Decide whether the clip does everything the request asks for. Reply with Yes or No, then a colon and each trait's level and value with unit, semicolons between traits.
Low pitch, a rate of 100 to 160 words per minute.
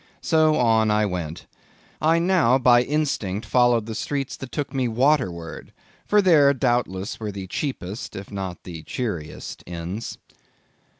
Yes: low, 115 Hz; average, 140 wpm